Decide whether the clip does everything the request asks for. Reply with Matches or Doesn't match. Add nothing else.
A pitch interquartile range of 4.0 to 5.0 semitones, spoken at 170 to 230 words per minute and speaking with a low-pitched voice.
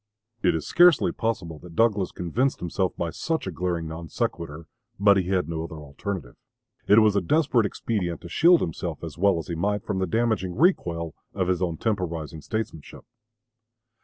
Matches